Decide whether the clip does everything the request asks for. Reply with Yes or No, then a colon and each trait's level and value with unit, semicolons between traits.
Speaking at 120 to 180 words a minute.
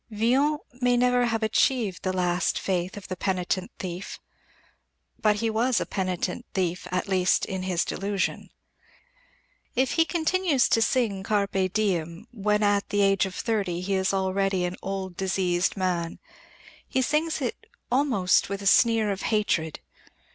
Yes: average, 155 wpm